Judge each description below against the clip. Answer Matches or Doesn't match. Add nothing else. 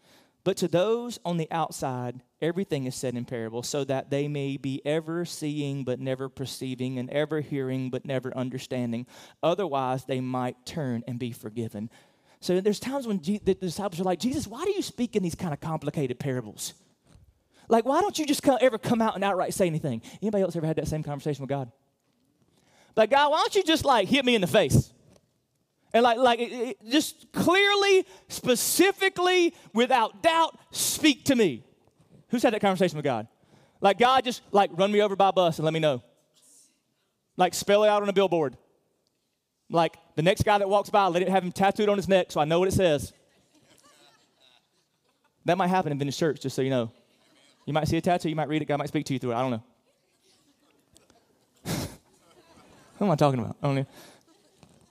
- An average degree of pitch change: Doesn't match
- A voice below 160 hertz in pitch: Doesn't match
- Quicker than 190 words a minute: Matches